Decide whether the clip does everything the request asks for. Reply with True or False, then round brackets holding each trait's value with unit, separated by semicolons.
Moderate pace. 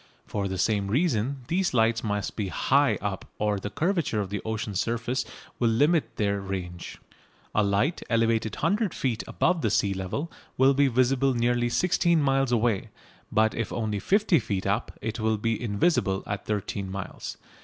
True (170 wpm)